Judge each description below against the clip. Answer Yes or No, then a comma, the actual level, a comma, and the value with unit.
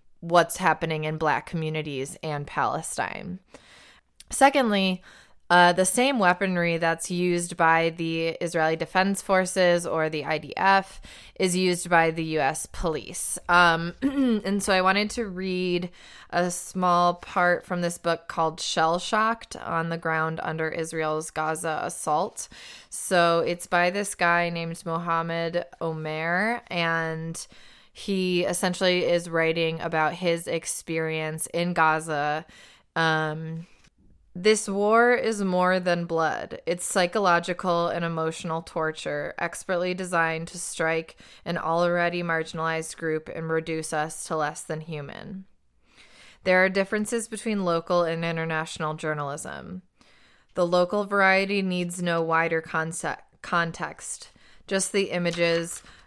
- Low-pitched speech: No, medium, 170 Hz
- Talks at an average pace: No, slow, 125 wpm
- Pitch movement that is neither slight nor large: No, narrow, 2.2 semitones